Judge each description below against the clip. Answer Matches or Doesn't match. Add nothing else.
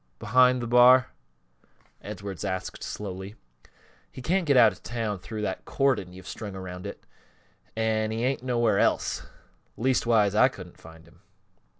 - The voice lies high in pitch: Doesn't match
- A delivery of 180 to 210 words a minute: Doesn't match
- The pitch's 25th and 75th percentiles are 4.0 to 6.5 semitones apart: Matches